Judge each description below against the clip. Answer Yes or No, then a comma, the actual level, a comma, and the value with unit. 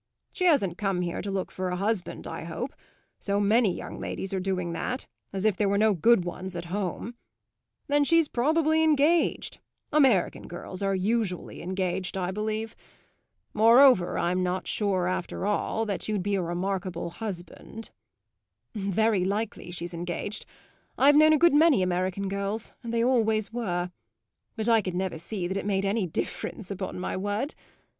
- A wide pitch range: No, average, 3.7 semitones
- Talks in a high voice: Yes, high, 200 Hz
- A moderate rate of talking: Yes, average, 165 wpm